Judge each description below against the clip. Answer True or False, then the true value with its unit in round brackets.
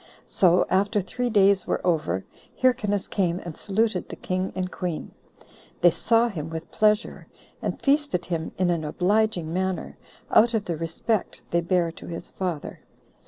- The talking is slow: False (160 wpm)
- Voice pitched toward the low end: False (185 Hz)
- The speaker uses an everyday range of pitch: True (3.9 semitones)